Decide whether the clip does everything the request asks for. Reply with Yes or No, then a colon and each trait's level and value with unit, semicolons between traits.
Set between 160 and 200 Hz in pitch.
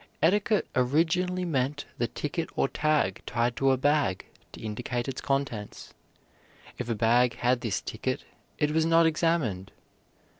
No: low, 135 Hz